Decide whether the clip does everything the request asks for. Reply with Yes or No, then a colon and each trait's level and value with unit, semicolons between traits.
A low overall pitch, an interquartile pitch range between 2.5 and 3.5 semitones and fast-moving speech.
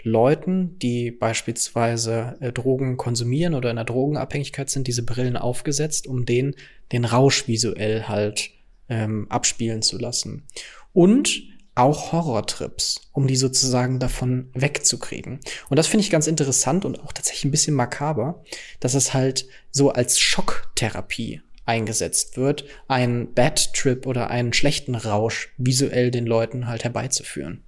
No: low, 125 Hz; average, 3.2 semitones; average, 135 wpm